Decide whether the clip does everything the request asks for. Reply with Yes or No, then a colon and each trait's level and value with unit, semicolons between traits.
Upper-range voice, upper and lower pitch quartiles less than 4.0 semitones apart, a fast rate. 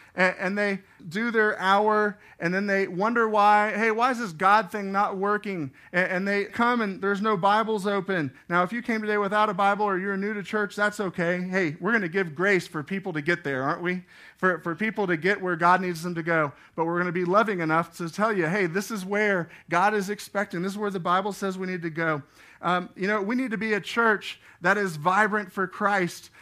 Yes: high, 195 Hz; average, 2.8 semitones; fast, 240 wpm